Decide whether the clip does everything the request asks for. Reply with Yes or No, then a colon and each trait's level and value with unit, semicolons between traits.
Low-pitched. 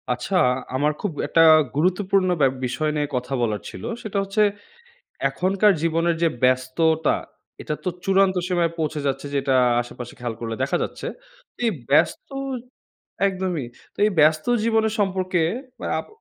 No: medium, 165 Hz